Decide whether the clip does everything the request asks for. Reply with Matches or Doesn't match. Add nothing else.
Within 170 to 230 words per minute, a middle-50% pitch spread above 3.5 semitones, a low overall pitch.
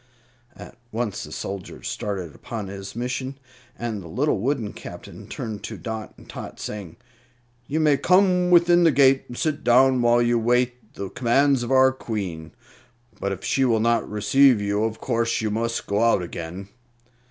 Matches